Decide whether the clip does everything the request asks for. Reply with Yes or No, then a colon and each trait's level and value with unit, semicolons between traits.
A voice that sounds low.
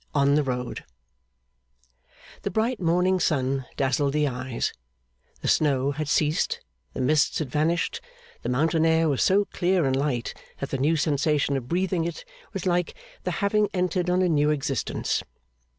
No: medium, 150 Hz